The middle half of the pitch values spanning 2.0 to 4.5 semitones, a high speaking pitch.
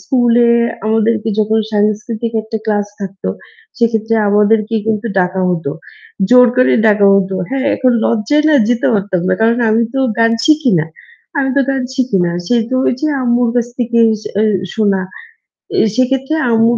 Yes: average, 2.9 semitones; high, 225 Hz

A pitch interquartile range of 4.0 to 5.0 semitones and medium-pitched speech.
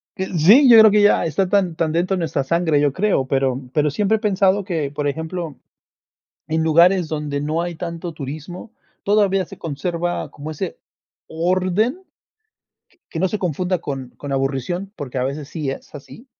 Yes: average, 4.4 semitones; medium, 170 Hz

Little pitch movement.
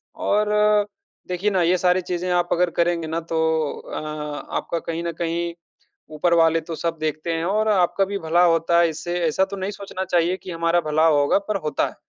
Yes: narrow, 1.8 semitones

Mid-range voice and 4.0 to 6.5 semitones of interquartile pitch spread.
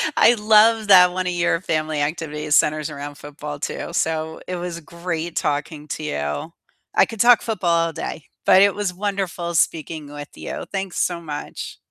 No: medium, 170 Hz; average, 3.5 semitones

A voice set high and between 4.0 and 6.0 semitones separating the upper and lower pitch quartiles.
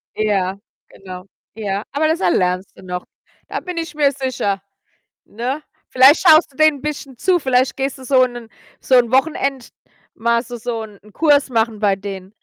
Yes: high, 245 Hz; wide, 5.5 semitones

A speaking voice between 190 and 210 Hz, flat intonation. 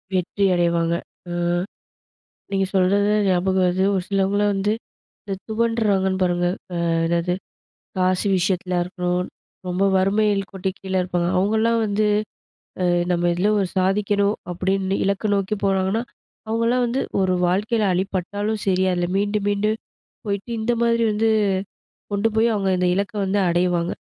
Yes: high, 195 Hz; narrow, 2.3 semitones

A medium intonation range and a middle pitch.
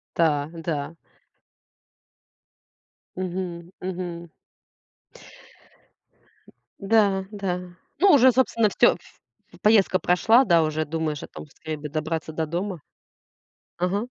Yes: average, 3.7 semitones; medium, 175 Hz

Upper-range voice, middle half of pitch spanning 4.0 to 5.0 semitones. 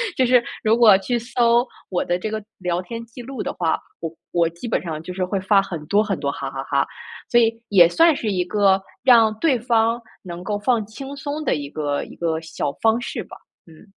No: high, 205 Hz; wide, 5.5 semitones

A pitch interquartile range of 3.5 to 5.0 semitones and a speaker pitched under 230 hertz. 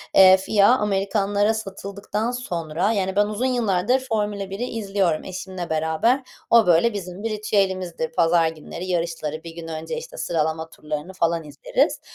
Yes: average, 4.0 semitones; high, 190 Hz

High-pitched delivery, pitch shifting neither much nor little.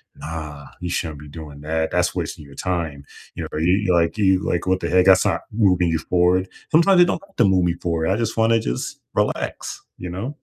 No: very low, 90 Hz; average, 3.2 semitones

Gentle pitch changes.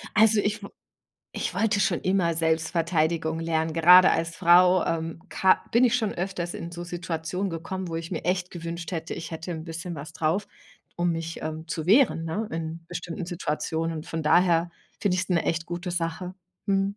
Yes: narrow, 2.0 semitones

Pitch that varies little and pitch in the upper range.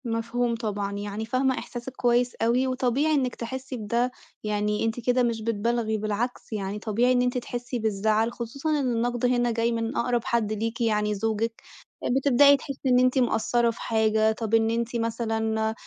Yes: narrow, 2.1 semitones; high, 235 Hz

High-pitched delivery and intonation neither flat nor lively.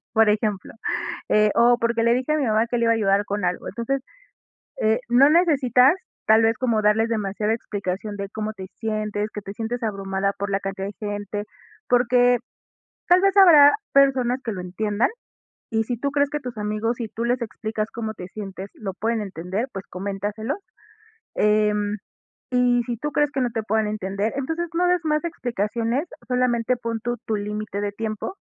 Yes: high, 225 Hz; average, 3.2 semitones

